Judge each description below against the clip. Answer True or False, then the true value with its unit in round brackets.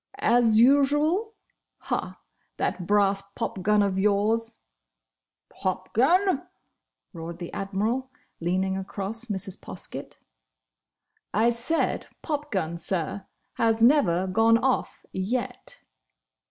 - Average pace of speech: False (85 wpm)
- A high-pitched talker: True (215 Hz)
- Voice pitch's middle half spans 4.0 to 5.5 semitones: True (4.7 semitones)